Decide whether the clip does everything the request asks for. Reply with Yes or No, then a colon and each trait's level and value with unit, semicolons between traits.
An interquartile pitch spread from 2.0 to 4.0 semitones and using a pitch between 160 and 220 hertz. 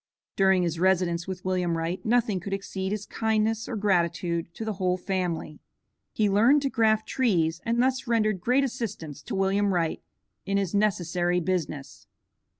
Yes: average, 3.7 semitones; high, 190 Hz